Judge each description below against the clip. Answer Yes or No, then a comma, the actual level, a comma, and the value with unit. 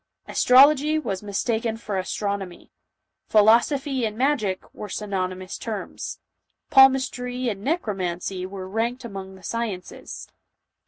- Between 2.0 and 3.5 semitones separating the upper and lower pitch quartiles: No, average, 4.6 semitones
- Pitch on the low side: No, high, 215 Hz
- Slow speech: Yes, slow, 115 wpm